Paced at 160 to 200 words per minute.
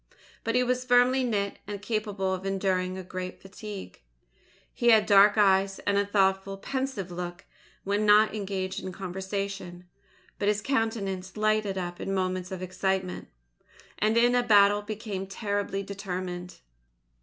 No: average, 140 wpm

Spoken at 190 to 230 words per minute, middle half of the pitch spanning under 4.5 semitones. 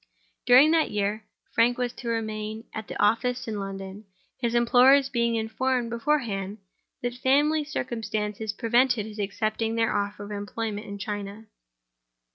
No: average, 140 wpm; average, 2.8 semitones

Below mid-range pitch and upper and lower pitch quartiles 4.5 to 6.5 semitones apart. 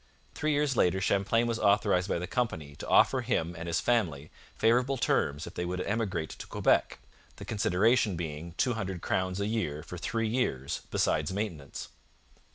Yes: very low, 95 Hz; average, 5.3 semitones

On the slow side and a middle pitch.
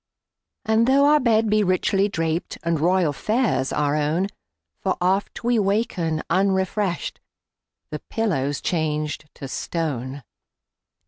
Yes: slow, 105 wpm; medium, 180 Hz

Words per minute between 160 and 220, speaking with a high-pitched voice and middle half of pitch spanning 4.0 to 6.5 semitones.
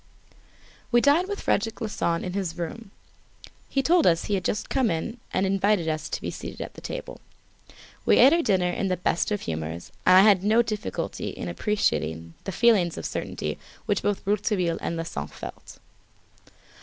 Yes: average, 180 wpm; high, 195 Hz; average, 4.9 semitones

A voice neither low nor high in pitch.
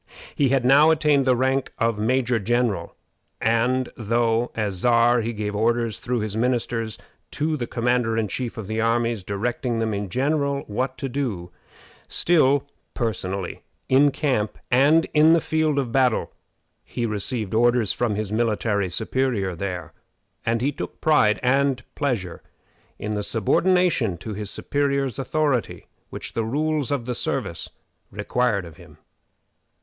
No: low, 120 Hz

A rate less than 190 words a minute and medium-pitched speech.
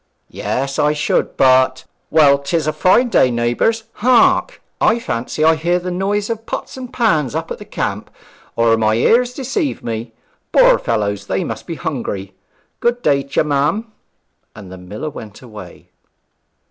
Yes: average, 160 wpm; medium, 150 Hz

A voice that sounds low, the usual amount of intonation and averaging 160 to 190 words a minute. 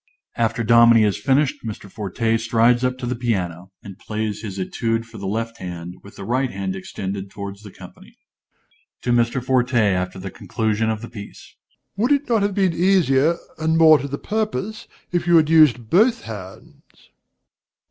No: low, 115 Hz; wide, 6.3 semitones; average, 180 wpm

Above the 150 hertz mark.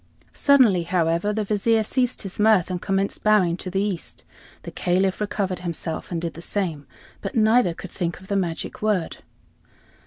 Yes: high, 190 Hz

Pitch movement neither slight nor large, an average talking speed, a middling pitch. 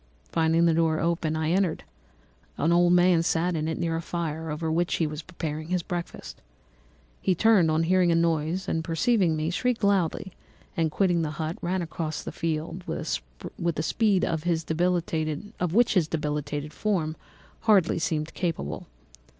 No: narrow, 2.1 semitones; average, 160 wpm; medium, 165 Hz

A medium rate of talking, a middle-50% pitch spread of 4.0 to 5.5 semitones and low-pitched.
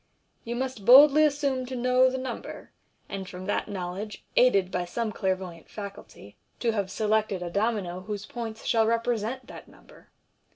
No: average, 160 wpm; average, 4.6 semitones; high, 220 Hz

